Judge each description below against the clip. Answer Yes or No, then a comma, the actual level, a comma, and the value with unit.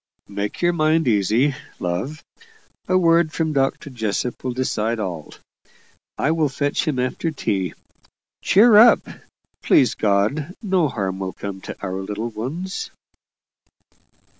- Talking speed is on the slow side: Yes, slow, 130 wpm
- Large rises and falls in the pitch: Yes, wide, 7.9 semitones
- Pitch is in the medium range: No, low, 130 Hz